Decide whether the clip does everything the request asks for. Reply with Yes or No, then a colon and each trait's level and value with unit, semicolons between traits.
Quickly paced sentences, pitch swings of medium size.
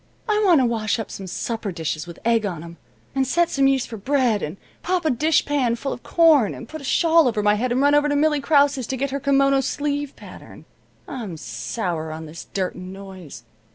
No: fast, 225 wpm; wide, 6.9 semitones